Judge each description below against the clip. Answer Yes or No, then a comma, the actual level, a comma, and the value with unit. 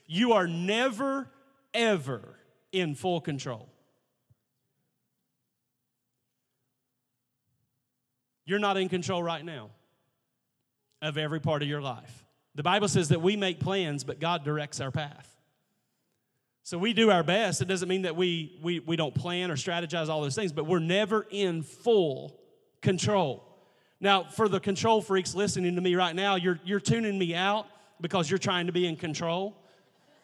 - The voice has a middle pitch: Yes, medium, 170 Hz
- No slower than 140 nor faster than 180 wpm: Yes, average, 155 wpm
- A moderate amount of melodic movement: No, wide, 6.4 semitones